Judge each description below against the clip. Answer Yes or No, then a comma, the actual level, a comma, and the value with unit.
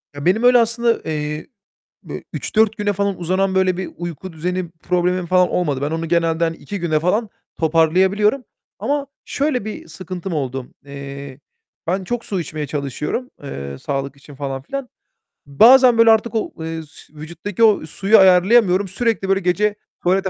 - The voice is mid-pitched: Yes, medium, 180 Hz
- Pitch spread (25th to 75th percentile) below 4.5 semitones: No, average, 5.1 semitones